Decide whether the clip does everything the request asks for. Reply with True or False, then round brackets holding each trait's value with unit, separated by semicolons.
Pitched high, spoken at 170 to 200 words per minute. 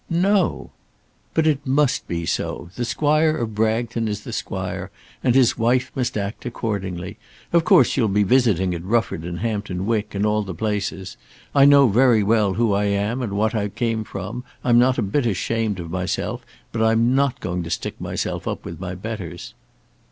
False (110 Hz; 190 wpm)